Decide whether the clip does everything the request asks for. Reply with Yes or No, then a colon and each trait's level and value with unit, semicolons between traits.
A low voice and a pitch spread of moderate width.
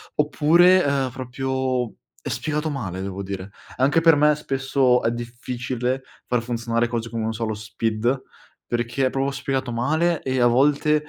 Yes: low, 130 Hz; average, 3.2 semitones